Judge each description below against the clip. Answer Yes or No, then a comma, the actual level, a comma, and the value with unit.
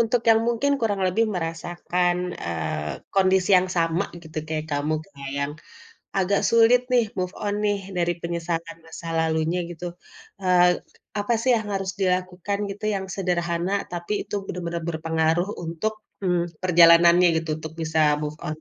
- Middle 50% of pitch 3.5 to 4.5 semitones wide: No, average, 2.9 semitones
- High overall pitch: No, medium, 175 Hz